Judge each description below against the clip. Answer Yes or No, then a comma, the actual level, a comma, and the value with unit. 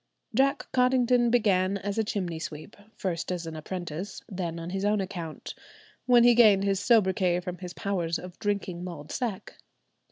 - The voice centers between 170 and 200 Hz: Yes, high, 190 Hz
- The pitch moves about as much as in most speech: Yes, average, 3.5 semitones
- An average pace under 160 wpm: No, average, 165 wpm